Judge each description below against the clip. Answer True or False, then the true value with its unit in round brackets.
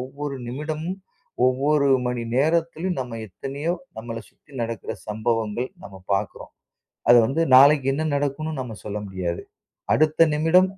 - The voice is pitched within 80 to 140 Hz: True (135 Hz)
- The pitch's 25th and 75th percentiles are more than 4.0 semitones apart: True (5.0 semitones)